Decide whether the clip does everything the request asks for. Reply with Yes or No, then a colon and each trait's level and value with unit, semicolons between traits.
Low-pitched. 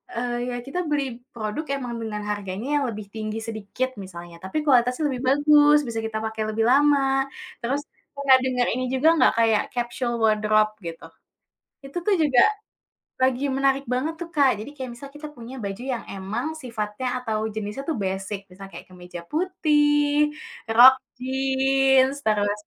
No: very high, 250 Hz